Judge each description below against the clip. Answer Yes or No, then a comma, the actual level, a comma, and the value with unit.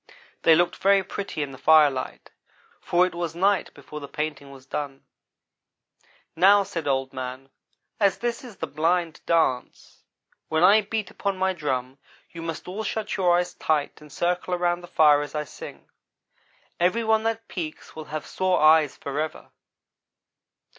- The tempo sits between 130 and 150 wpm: No, average, 160 wpm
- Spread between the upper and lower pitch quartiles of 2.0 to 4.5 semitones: Yes, average, 4.2 semitones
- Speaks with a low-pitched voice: No, medium, 165 Hz